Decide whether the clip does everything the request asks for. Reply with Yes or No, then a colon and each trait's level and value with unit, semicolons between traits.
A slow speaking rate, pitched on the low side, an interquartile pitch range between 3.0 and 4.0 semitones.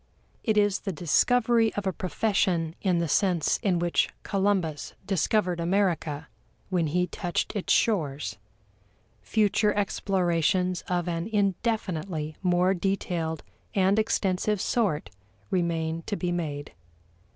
No: slow, 120 wpm; medium, 180 Hz; average, 3.4 semitones